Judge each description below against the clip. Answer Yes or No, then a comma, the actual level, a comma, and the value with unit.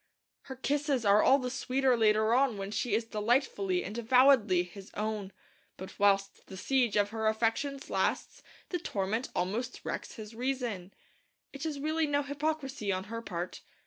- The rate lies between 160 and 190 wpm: Yes, average, 165 wpm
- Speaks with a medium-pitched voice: No, high, 230 Hz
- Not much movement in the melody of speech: No, average, 4.9 semitones